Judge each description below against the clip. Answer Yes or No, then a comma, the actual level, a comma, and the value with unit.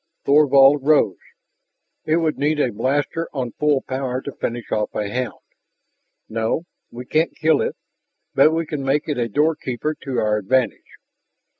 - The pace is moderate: Yes, average, 155 wpm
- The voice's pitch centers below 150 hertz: Yes, low, 135 Hz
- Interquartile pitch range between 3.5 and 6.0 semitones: Yes, average, 3.9 semitones